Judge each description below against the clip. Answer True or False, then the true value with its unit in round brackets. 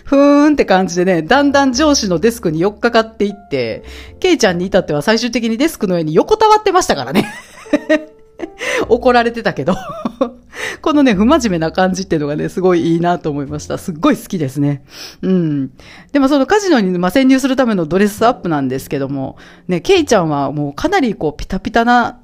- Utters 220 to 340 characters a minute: False (415 characters per minute)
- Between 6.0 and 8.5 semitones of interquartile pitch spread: True (8.1 semitones)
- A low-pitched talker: False (220 Hz)